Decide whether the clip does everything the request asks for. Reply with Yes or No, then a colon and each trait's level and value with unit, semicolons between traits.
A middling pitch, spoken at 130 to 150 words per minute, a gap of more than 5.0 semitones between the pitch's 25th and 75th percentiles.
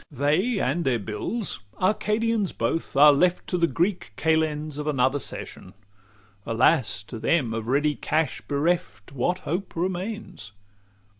Yes: medium, 155 Hz; average, 140 wpm; wide, 5.6 semitones